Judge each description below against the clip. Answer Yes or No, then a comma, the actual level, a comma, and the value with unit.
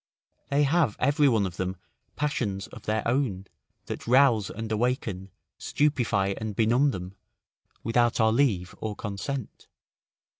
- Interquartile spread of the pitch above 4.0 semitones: Yes, average, 5.3 semitones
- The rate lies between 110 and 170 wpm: Yes, slow, 135 wpm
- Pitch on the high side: No, low, 115 Hz